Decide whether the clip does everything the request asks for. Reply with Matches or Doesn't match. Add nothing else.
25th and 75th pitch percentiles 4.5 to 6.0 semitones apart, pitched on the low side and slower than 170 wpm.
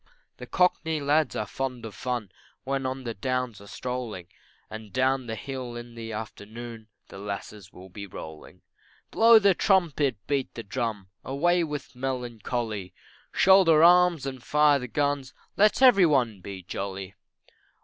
Matches